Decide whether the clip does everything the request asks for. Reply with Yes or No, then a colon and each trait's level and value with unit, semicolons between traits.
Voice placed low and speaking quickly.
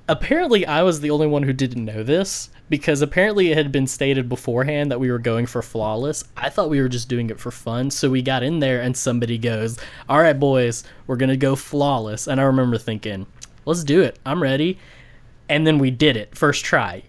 Yes: low, 130 Hz; fast, 220 wpm